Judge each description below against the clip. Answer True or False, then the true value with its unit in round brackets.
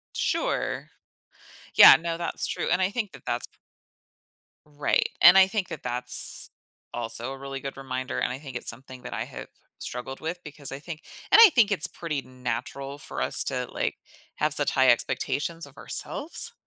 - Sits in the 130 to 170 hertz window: True (140 Hz)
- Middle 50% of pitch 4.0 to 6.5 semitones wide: True (4.7 semitones)